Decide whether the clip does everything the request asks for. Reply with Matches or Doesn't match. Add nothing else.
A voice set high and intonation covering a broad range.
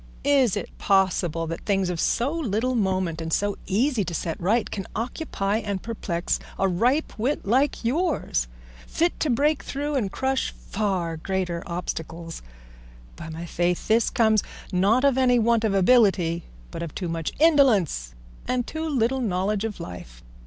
Matches